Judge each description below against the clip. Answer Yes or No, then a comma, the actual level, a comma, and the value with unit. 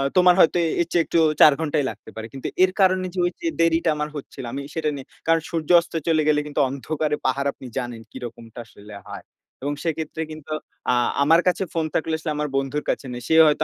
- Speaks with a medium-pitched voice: Yes, medium, 155 Hz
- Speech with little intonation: No, average, 3.2 semitones